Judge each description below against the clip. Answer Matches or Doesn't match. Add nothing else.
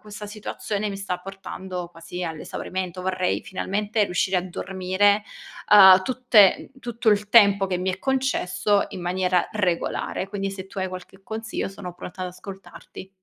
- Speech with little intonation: Matches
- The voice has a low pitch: Doesn't match